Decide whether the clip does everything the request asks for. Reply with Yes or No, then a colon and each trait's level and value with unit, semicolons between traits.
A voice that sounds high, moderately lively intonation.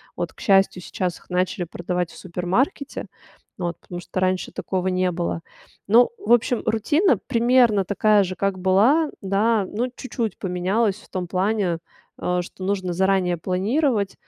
Yes: high, 195 Hz; average, 3.7 semitones